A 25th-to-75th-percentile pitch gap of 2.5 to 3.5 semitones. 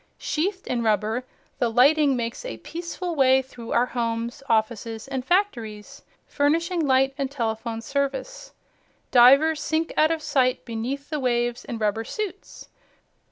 No: average, 5.0 semitones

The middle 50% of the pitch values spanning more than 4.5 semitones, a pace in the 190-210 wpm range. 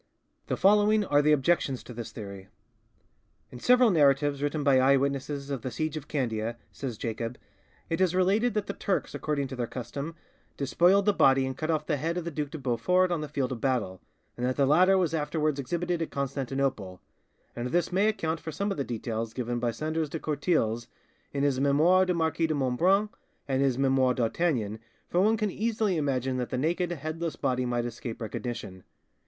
Yes: average, 5.1 semitones; average, 200 wpm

